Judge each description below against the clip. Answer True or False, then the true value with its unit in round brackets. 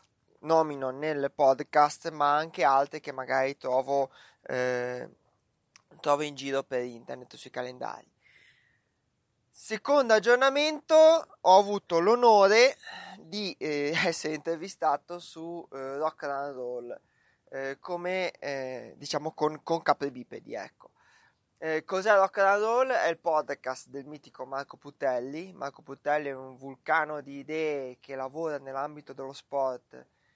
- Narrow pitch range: False (3.9 semitones)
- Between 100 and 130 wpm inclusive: True (120 wpm)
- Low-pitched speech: False (150 Hz)